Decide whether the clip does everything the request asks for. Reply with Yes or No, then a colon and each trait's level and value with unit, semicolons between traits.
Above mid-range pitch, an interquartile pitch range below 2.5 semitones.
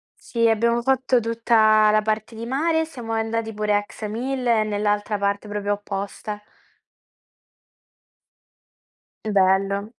Yes: high, 215 Hz; narrow, 2.1 semitones